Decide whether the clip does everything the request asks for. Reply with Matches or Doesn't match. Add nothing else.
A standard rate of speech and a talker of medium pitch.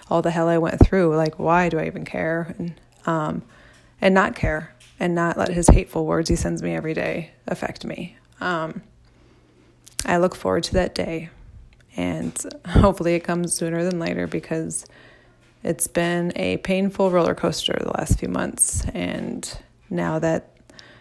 Matches